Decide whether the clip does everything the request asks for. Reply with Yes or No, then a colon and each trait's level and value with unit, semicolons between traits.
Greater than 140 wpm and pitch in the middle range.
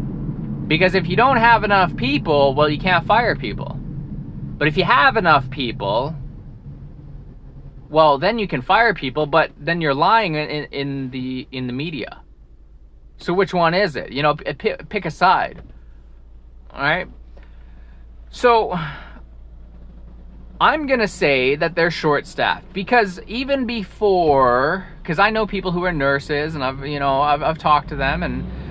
Yes: average, 155 wpm; medium, 145 Hz